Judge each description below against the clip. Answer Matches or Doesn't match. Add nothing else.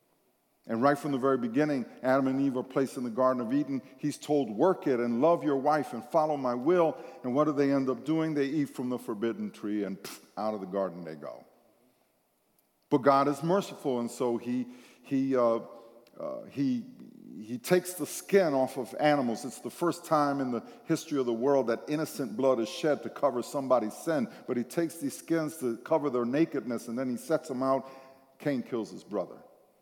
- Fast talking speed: Matches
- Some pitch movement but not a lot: Matches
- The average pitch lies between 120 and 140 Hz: Matches